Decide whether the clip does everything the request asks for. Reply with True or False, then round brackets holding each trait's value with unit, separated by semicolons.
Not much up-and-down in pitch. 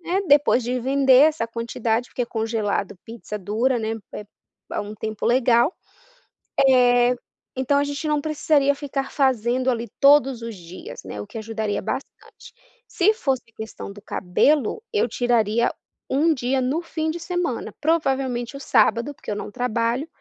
False (3.9 semitones)